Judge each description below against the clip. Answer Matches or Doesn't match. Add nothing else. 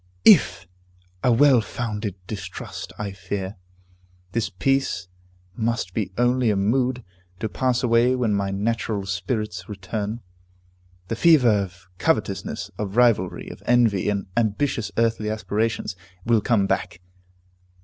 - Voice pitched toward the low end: Matches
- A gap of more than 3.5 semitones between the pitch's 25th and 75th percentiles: Doesn't match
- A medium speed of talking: Doesn't match